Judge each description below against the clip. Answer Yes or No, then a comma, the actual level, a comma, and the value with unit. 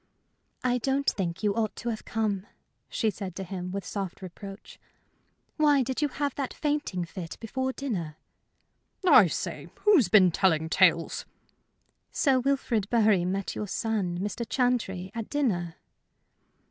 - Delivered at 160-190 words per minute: No, average, 145 wpm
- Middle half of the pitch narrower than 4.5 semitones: No, wide, 5.6 semitones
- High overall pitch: Yes, high, 210 Hz